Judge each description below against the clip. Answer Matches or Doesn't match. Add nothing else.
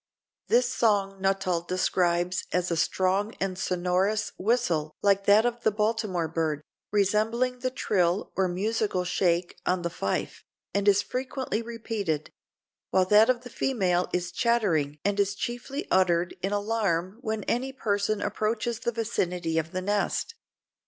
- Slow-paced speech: Doesn't match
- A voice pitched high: Matches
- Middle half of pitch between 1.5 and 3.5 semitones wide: Doesn't match